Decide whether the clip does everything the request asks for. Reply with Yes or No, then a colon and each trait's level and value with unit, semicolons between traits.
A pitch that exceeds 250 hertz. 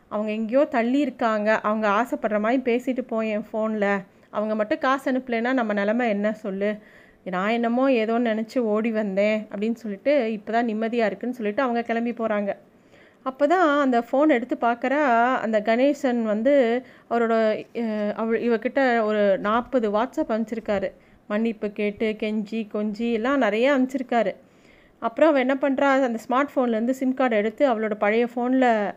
No: high, 230 Hz